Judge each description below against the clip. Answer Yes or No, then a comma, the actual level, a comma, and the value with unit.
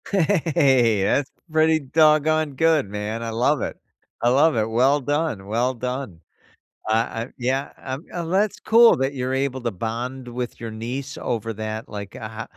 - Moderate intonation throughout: Yes, average, 4.7 semitones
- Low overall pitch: Yes, low, 130 Hz